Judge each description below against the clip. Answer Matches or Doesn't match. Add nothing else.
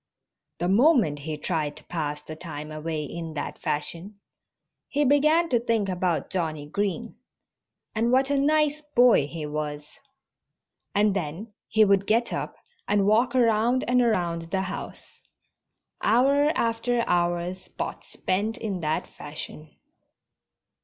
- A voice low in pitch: Doesn't match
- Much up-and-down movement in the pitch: Matches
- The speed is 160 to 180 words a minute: Doesn't match